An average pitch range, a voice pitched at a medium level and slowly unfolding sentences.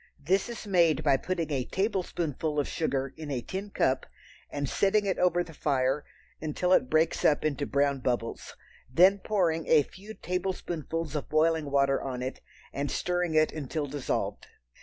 No: average, 4.2 semitones; medium, 155 Hz; average, 165 wpm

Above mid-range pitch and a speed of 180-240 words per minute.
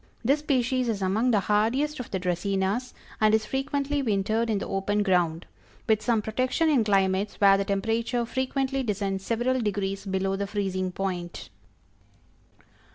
No: high, 210 Hz; average, 155 wpm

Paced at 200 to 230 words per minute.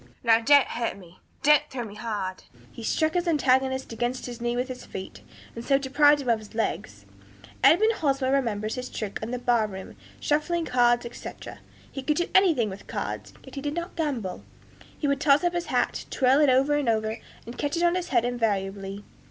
Yes: fast, 205 wpm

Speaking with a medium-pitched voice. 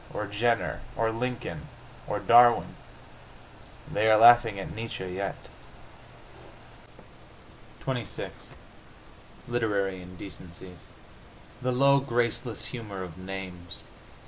No: low, 105 Hz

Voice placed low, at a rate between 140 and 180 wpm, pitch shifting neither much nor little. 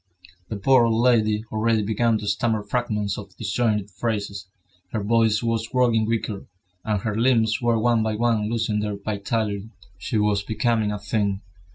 No: low, 110 Hz; average, 165 wpm; narrow, 1.8 semitones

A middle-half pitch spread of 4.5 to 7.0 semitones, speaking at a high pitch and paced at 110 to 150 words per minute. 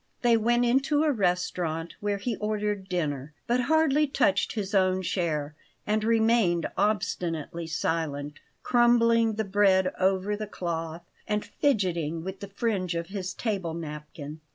Yes: average, 4.8 semitones; high, 195 Hz; average, 140 wpm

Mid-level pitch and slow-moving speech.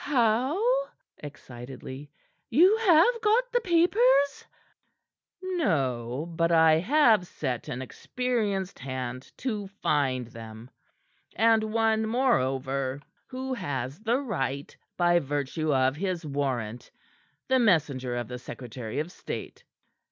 Yes: medium, 165 Hz; slow, 110 wpm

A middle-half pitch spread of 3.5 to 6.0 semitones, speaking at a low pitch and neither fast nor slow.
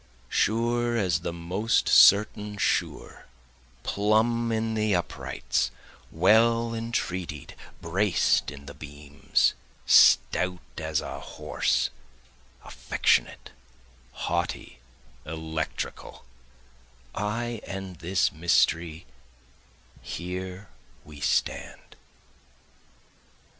No: average, 5.0 semitones; very low, 95 Hz; slow, 75 wpm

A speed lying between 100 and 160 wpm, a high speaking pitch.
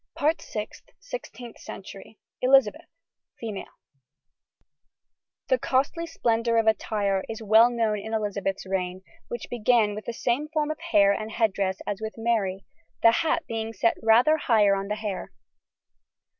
Yes: average, 140 wpm; high, 220 Hz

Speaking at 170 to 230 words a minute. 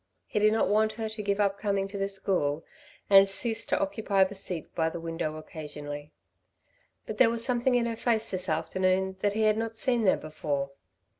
Yes: fast, 205 wpm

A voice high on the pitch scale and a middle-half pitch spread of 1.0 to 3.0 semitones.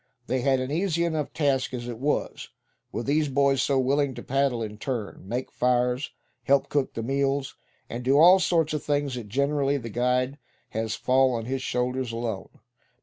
No: low, 130 Hz; narrow, 2.5 semitones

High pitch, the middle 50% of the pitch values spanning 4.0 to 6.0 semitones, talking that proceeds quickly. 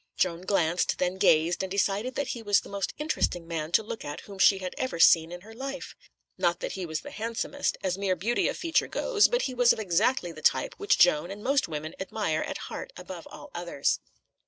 Yes: high, 195 Hz; average, 5.3 semitones; fast, 225 wpm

